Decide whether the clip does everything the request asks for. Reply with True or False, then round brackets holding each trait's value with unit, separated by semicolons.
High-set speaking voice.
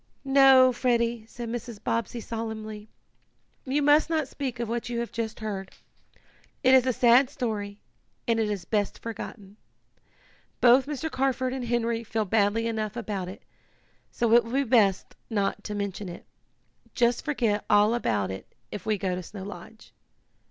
True (230 Hz)